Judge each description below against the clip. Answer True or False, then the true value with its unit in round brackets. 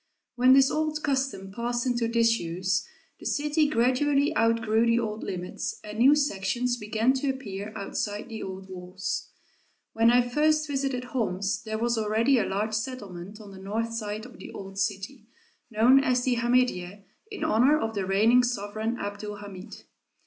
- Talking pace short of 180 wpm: True (165 wpm)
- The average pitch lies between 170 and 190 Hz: False (230 Hz)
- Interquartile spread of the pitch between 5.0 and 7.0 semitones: False (3.8 semitones)